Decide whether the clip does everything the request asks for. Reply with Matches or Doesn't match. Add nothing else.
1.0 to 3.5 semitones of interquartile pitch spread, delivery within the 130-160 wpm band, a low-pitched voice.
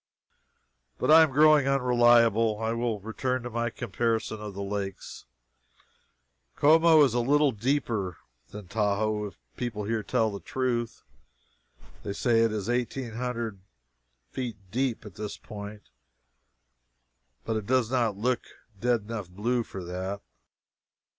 Matches